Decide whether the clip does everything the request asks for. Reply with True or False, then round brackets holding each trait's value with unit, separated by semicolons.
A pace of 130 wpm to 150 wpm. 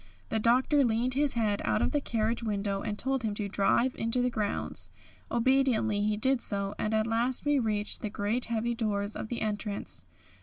False (195 wpm)